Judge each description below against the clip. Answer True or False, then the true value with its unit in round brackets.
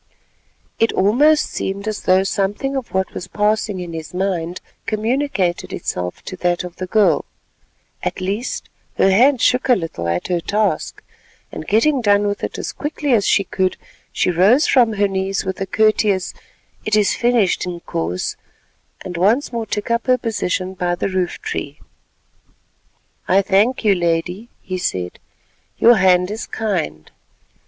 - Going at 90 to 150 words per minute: False (160 wpm)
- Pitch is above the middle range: True (195 Hz)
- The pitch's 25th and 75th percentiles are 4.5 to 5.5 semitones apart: False (3.6 semitones)